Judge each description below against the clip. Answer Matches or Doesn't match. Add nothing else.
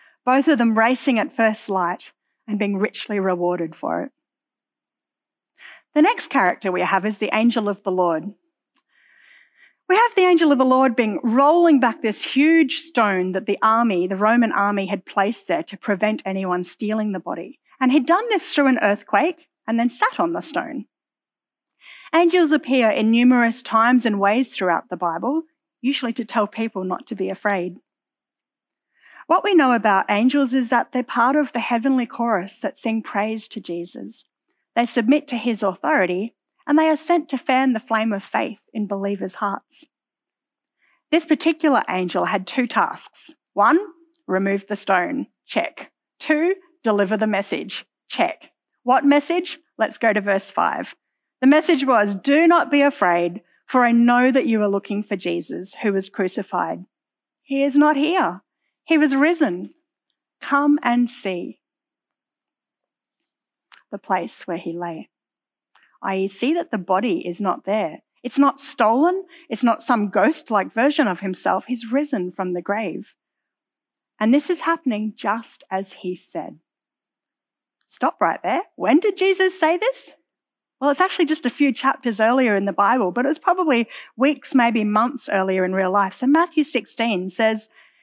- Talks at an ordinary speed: Matches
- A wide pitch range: Matches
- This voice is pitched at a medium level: Doesn't match